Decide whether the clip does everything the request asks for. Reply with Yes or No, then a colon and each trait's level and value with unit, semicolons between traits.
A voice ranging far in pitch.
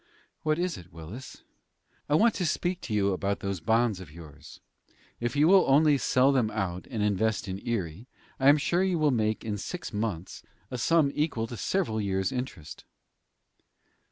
Yes: wide, 7.0 semitones